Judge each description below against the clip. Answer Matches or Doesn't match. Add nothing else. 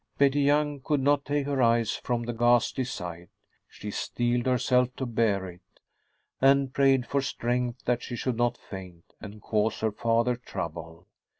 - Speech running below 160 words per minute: Doesn't match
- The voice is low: Matches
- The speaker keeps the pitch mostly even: Doesn't match